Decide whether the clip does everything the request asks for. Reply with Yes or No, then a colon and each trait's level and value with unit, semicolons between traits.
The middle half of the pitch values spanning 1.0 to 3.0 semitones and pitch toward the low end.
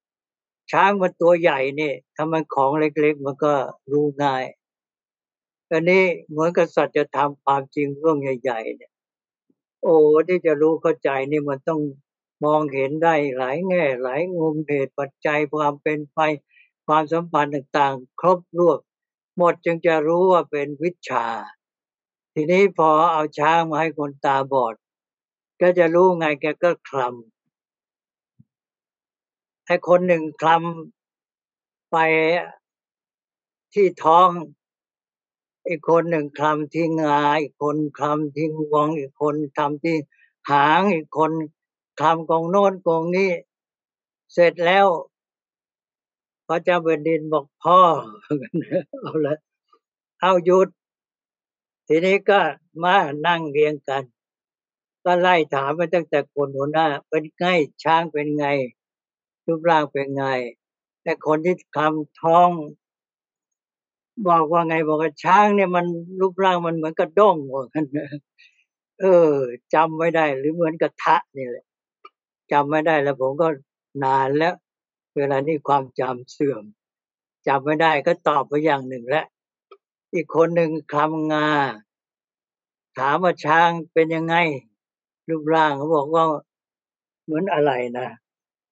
No: average, 2.7 semitones; medium, 155 Hz